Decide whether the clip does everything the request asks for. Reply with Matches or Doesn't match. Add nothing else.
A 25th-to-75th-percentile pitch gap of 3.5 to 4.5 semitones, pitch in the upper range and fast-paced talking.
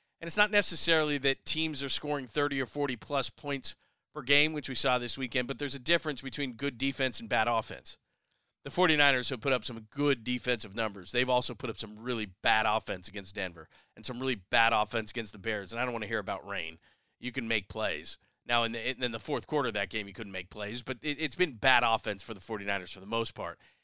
Doesn't match